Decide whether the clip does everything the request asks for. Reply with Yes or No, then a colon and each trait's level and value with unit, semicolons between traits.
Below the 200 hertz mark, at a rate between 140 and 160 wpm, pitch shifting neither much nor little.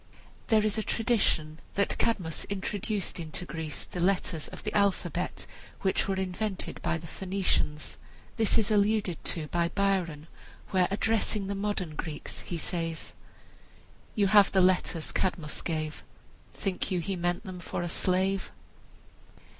Yes: medium, 185 Hz; average, 145 wpm; average, 3.0 semitones